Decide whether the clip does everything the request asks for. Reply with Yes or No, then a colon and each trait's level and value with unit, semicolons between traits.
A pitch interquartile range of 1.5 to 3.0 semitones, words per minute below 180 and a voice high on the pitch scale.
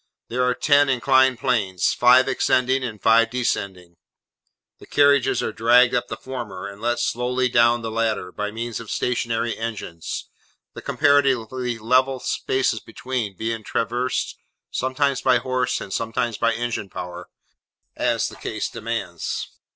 No: narrow, 2.6 semitones; average, 145 wpm; low, 120 Hz